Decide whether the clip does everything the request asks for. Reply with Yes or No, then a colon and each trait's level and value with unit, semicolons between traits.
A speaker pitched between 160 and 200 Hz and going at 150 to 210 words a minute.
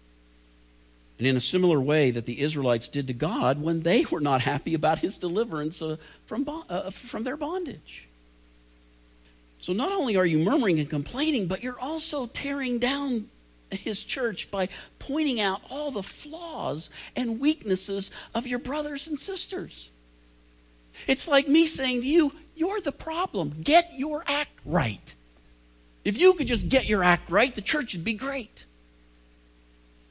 Yes: medium, 185 Hz; average, 160 wpm